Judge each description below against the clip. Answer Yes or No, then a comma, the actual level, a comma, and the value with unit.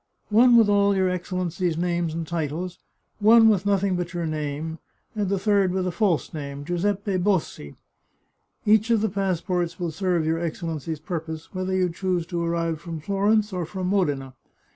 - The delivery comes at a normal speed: Yes, average, 170 wpm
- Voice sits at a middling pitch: Yes, medium, 180 Hz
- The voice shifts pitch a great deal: No, average, 3.3 semitones